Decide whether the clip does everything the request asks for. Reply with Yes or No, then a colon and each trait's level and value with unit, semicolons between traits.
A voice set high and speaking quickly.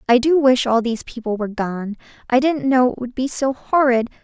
Yes: very high, 250 Hz; fast, 240 wpm